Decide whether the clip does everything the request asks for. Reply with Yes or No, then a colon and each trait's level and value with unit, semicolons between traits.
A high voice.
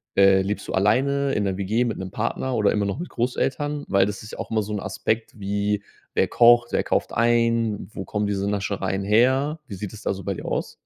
No: low, 105 Hz